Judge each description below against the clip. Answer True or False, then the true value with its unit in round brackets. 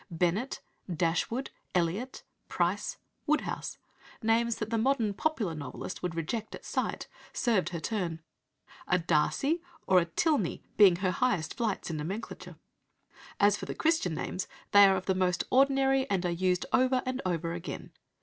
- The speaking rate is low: False (155 wpm)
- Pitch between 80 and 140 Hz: False (195 Hz)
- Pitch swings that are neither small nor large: False (6.1 semitones)